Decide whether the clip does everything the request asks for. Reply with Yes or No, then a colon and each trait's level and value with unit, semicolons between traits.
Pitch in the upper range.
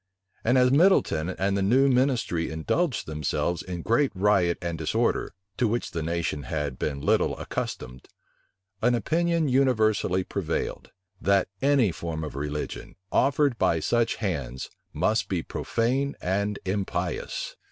No: low, 100 Hz